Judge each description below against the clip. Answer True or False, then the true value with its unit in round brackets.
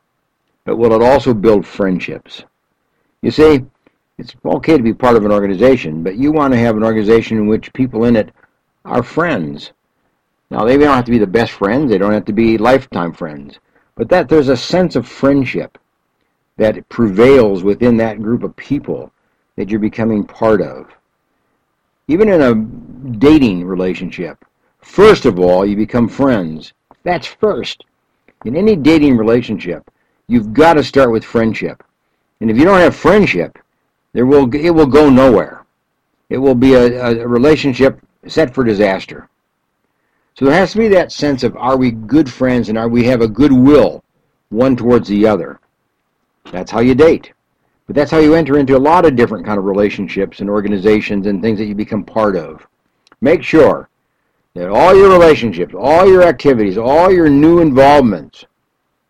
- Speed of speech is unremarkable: True (175 wpm)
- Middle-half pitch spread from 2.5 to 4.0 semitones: False (4.9 semitones)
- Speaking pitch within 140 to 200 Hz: False (120 Hz)